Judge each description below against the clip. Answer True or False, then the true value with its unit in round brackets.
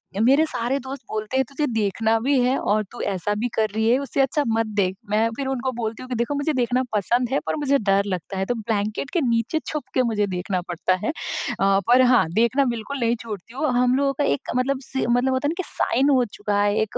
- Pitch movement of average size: True (4.0 semitones)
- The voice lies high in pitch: True (240 Hz)